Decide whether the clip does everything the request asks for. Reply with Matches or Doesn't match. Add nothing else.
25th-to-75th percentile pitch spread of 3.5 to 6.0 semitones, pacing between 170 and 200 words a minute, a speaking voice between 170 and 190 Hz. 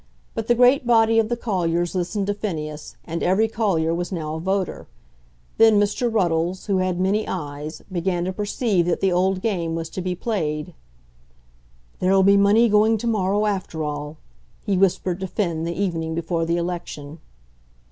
Matches